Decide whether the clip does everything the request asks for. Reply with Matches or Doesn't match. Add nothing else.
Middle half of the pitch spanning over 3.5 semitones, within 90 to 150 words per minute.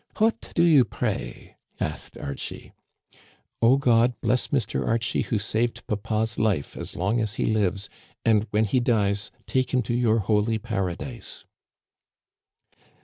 Doesn't match